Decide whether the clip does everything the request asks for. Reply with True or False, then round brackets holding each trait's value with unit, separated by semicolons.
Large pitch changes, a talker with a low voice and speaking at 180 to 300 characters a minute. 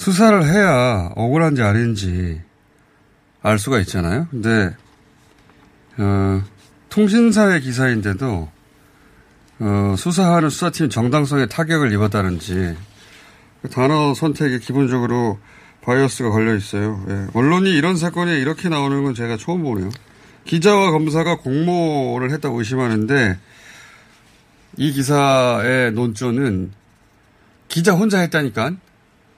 True (6.7 semitones; 130 Hz; 260 characters per minute)